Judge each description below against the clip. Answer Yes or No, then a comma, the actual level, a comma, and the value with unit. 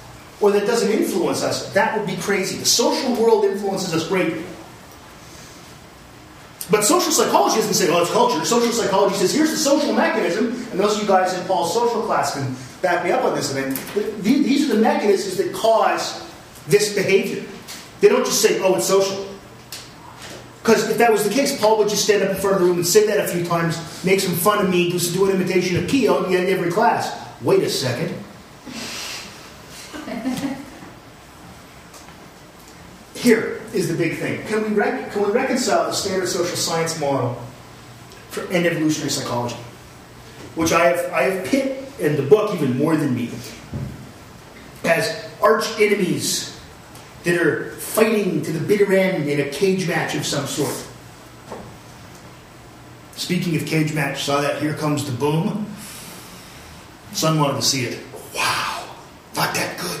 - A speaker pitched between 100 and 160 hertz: No, medium, 185 Hz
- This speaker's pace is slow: No, average, 170 wpm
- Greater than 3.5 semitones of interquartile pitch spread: Yes, average, 5.3 semitones